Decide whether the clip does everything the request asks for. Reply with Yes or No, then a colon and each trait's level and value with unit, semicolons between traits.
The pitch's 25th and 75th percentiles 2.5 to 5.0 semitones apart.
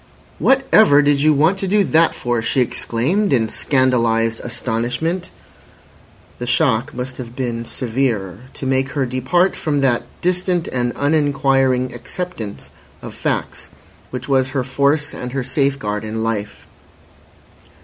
Yes: average, 3.6 semitones